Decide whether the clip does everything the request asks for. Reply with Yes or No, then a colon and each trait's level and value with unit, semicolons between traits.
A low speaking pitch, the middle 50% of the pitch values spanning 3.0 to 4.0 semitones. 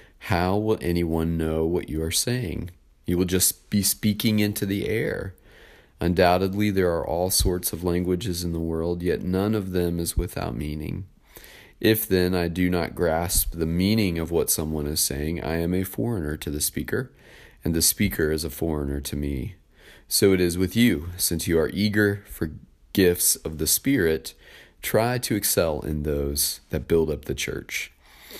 Yes: very low, 90 Hz; average, 3.7 semitones